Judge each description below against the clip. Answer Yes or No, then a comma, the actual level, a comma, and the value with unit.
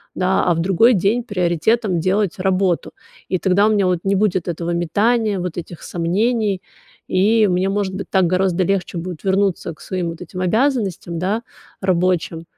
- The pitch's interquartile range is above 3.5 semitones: No, narrow, 2.6 semitones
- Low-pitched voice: No, medium, 185 Hz